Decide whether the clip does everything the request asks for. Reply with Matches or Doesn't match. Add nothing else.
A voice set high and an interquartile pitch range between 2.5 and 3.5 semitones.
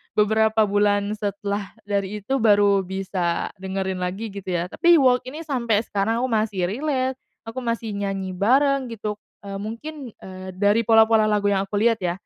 Matches